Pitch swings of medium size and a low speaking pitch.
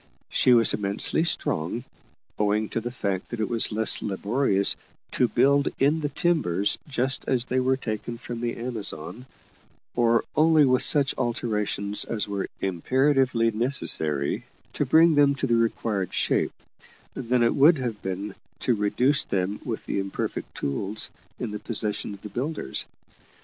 Yes: average, 4.3 semitones; low, 115 Hz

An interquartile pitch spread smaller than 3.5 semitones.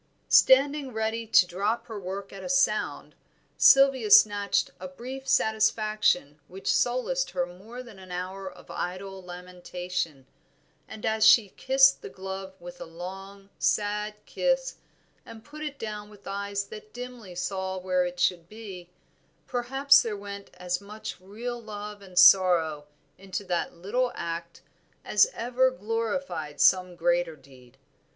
No: average, 4.0 semitones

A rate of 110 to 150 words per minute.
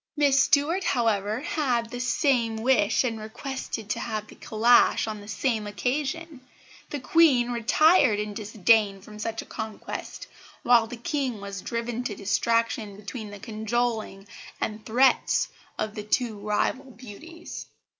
Yes: average, 145 wpm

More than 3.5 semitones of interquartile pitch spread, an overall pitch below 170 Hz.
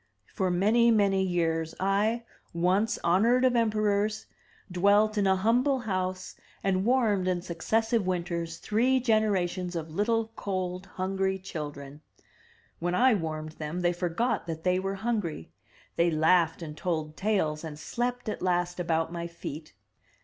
No: average, 4.1 semitones; medium, 185 Hz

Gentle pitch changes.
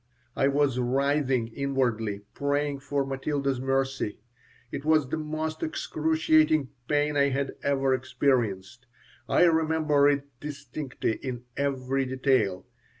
Yes: narrow, 2.2 semitones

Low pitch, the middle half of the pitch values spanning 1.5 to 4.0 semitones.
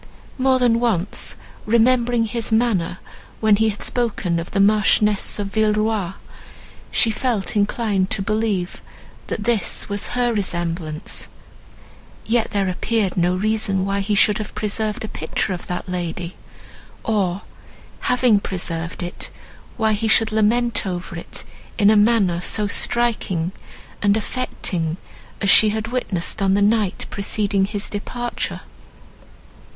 No: high, 210 Hz; average, 3.0 semitones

